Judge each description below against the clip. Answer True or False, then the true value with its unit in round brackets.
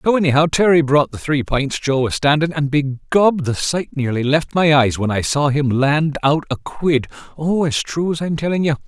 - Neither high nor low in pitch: True (150 Hz)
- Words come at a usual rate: False (225 wpm)